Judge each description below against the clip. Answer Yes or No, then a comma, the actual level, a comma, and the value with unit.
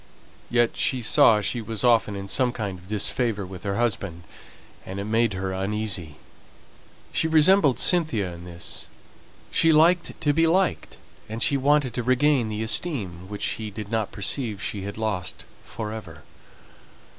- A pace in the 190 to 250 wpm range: No, average, 160 wpm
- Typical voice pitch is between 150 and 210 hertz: No, low, 110 Hz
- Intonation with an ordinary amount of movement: Yes, average, 4.8 semitones